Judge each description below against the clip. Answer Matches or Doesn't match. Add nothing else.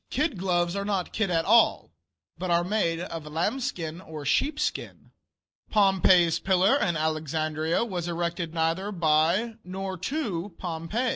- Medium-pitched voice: Matches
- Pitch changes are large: Doesn't match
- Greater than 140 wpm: Doesn't match